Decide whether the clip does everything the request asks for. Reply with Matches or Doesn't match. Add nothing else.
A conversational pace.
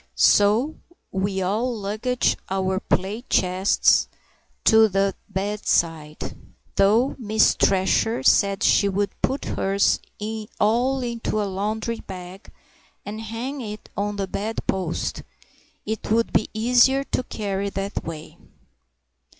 Doesn't match